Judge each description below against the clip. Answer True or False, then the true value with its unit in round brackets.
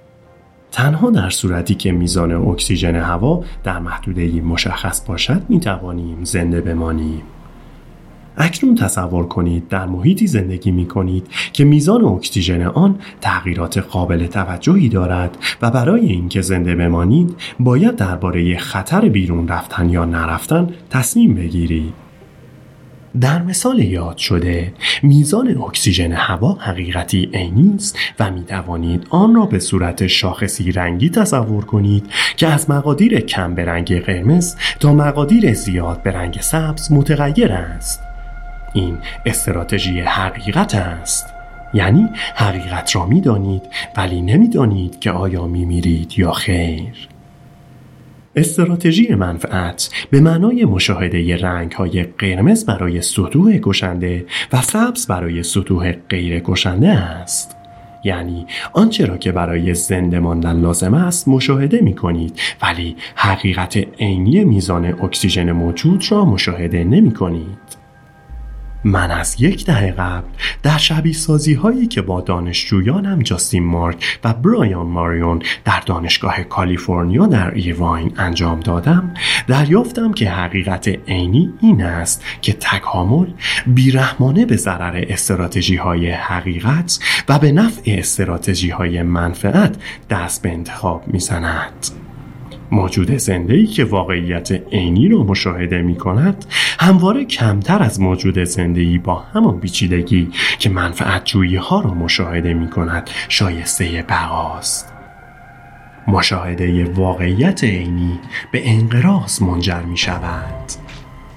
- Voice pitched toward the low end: True (95 Hz)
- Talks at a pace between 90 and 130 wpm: True (120 wpm)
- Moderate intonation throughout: False (7.1 semitones)